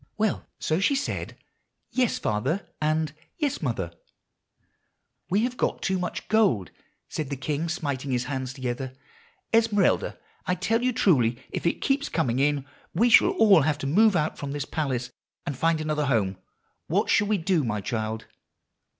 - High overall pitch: No, medium, 155 Hz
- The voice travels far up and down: Yes, wide, 7.3 semitones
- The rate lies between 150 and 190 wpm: Yes, average, 160 wpm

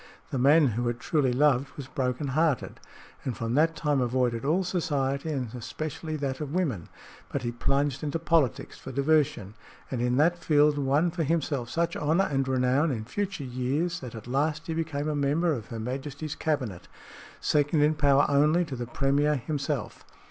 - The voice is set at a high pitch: No, medium, 140 Hz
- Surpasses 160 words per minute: Yes, average, 180 wpm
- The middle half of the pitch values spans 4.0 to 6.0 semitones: No, average, 3.5 semitones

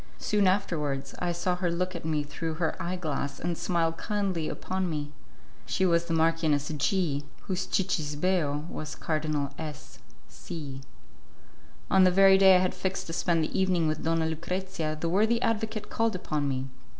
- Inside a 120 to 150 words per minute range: No, average, 170 wpm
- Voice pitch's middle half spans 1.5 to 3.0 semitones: No, average, 3.5 semitones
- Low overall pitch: No, medium, 170 Hz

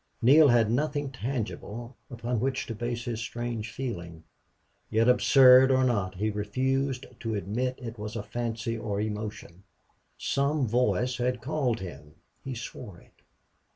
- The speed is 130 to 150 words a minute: Yes, average, 140 wpm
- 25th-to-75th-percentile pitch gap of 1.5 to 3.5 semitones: Yes, average, 3.1 semitones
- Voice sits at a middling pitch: No, low, 120 Hz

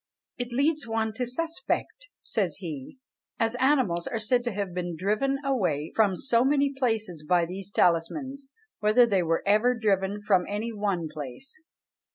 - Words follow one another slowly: No, average, 160 wpm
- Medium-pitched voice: No, high, 215 Hz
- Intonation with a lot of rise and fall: Yes, wide, 5.8 semitones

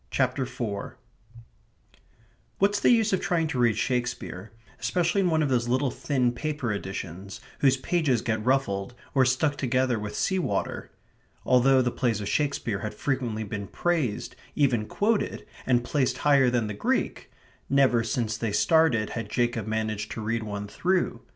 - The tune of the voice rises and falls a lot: No, average, 4.7 semitones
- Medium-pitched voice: No, low, 125 Hz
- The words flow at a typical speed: Yes, average, 160 wpm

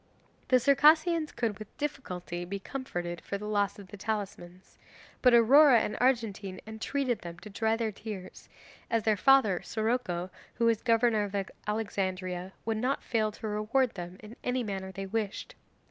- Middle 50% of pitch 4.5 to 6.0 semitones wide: No, average, 3.9 semitones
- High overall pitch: Yes, high, 215 Hz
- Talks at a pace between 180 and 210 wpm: No, average, 160 wpm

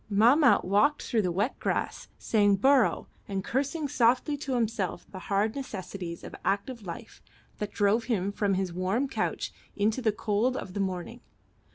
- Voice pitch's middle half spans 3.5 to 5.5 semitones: Yes, average, 4.6 semitones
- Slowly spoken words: No, average, 165 wpm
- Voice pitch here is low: No, high, 210 Hz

